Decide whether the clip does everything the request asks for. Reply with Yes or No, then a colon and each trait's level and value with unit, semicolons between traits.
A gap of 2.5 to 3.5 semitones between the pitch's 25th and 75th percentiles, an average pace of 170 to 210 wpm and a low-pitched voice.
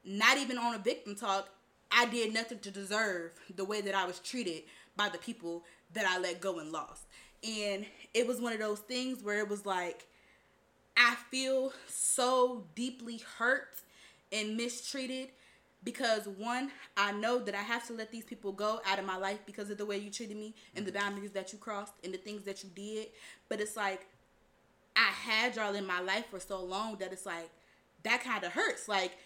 No: average, 3.2 semitones; fast, 205 wpm; high, 210 Hz